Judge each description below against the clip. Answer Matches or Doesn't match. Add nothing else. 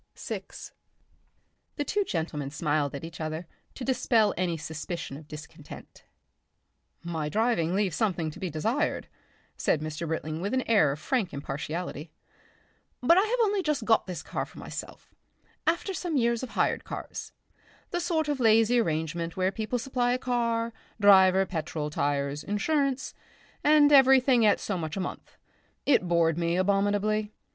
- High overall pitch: Matches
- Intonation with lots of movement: Matches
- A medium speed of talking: Matches